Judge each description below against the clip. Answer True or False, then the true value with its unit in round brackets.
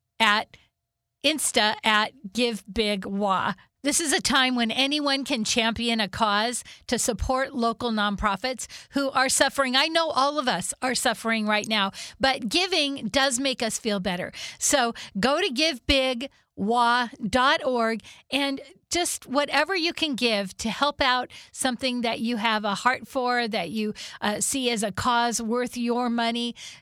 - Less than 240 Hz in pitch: False (245 Hz)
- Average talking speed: True (150 wpm)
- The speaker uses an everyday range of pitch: True (3.5 semitones)